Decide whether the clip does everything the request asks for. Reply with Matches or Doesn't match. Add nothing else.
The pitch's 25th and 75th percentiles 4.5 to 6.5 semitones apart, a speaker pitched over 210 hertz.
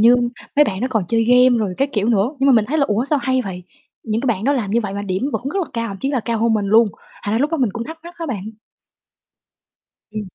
Doesn't match